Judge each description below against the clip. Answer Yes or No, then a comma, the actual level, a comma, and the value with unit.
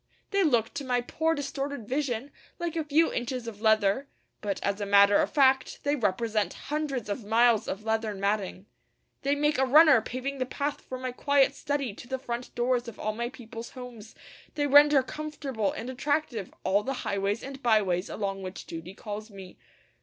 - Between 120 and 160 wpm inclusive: No, average, 185 wpm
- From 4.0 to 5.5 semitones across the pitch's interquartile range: Yes, average, 4.9 semitones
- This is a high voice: Yes, high, 245 Hz